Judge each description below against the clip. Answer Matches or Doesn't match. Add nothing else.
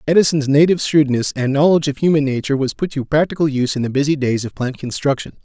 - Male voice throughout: Matches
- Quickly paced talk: Matches